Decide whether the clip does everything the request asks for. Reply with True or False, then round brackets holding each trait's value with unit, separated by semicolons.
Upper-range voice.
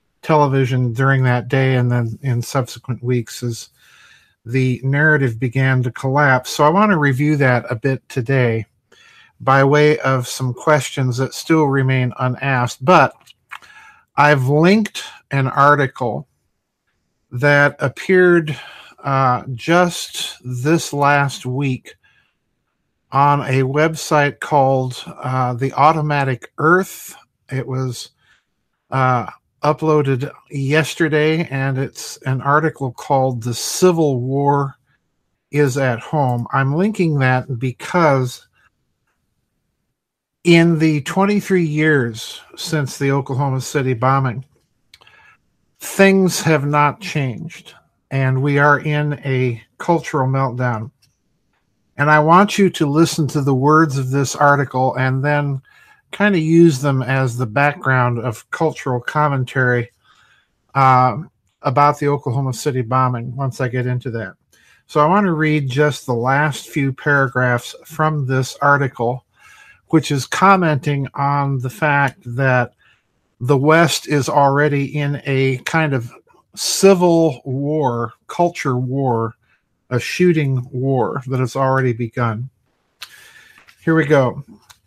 False (135 Hz)